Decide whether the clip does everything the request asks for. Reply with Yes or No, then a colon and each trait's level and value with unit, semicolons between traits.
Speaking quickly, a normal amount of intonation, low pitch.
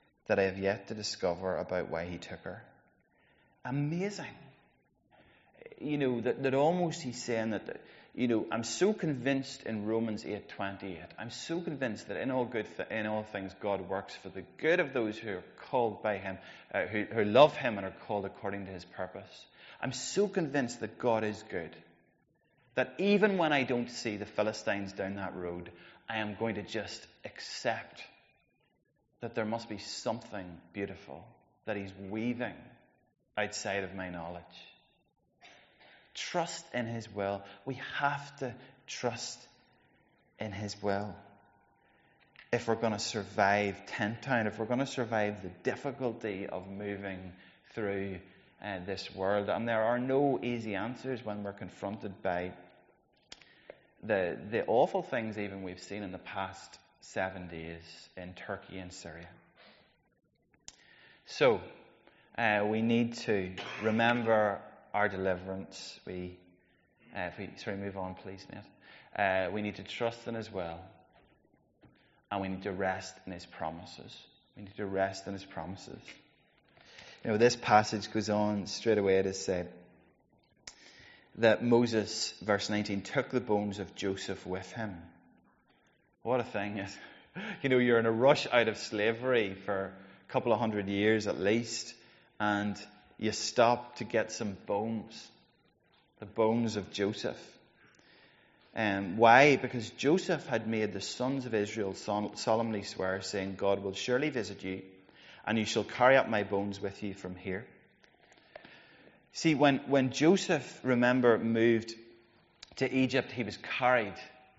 No: average, 150 wpm; average, 3.8 semitones; low, 105 Hz